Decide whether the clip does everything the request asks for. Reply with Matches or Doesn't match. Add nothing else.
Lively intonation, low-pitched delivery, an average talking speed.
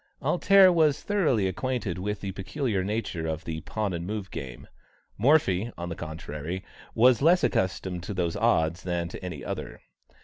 Matches